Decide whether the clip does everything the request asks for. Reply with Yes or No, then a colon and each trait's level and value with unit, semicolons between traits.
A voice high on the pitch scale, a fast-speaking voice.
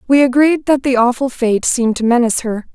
Yes: very high, 250 Hz; fast, 220 wpm